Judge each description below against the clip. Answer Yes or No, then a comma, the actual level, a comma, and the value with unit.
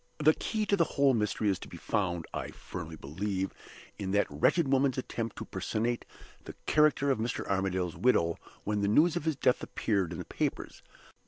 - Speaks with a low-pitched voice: Yes, low, 110 Hz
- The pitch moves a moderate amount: No, wide, 6.6 semitones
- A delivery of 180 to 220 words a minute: Yes, average, 190 wpm